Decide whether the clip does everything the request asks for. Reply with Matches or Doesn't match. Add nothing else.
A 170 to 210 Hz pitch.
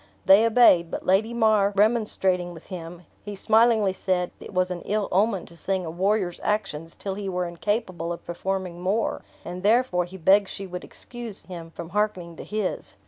Matches